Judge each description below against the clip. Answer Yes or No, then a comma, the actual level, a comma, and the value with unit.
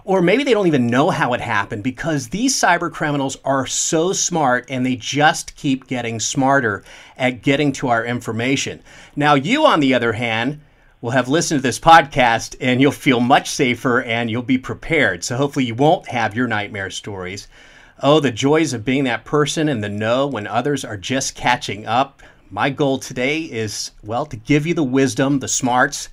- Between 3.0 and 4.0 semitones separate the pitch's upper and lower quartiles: Yes, average, 3.5 semitones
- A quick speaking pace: No, average, 195 wpm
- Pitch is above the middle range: No, low, 135 Hz